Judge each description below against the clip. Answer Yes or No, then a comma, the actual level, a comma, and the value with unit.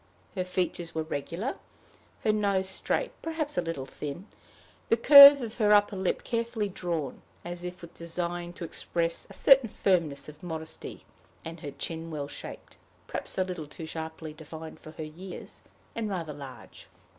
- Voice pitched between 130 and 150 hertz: No, medium, 175 Hz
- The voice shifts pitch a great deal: No, average, 4.1 semitones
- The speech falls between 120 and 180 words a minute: Yes, average, 165 wpm